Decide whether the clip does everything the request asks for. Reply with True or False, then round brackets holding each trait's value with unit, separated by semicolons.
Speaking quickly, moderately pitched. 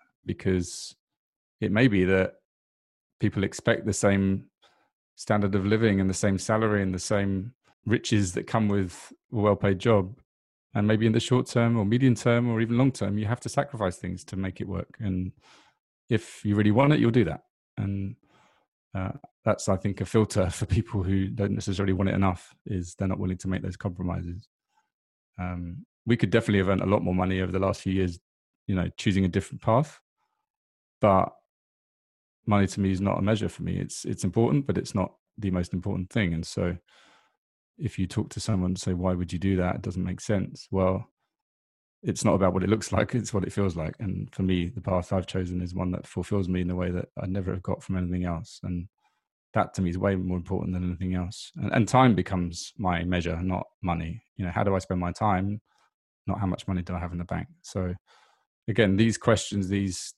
False (215 wpm; 95 Hz)